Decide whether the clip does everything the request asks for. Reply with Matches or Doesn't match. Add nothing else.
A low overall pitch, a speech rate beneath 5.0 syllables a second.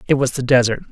Doesn't match